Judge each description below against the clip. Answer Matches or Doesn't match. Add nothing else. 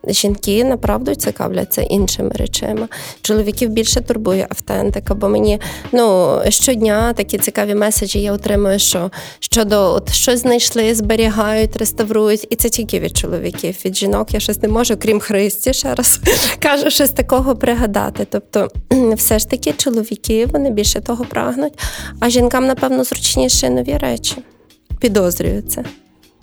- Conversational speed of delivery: Matches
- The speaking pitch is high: Matches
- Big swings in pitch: Doesn't match